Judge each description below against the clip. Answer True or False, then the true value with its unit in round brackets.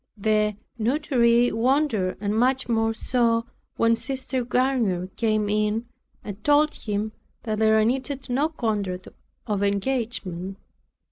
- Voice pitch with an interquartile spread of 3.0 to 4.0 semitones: True (3.3 semitones)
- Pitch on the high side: True (225 Hz)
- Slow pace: True (120 wpm)